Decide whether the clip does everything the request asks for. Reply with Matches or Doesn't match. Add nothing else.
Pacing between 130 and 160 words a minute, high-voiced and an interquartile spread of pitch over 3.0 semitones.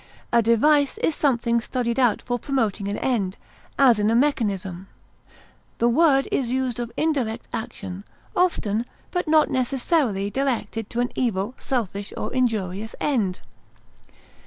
Matches